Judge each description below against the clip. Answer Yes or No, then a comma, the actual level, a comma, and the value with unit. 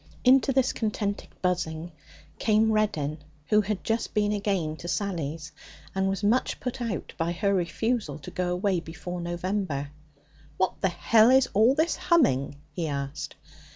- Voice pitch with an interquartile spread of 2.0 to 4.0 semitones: No, average, 4.7 semitones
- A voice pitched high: Yes, high, 195 Hz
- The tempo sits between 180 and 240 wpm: No, average, 155 wpm